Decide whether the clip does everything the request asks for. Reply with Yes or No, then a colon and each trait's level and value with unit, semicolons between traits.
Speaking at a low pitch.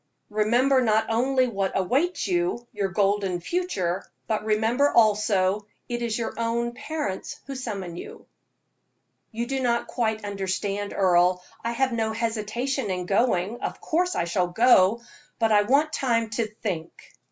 No: high, 220 Hz